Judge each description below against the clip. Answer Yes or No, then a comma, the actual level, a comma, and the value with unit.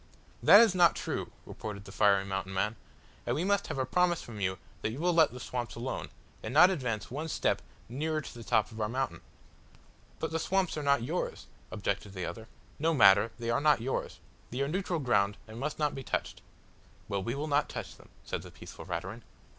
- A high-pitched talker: No, low, 130 Hz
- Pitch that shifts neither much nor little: No, wide, 6.5 semitones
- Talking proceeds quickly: Yes, fast, 215 wpm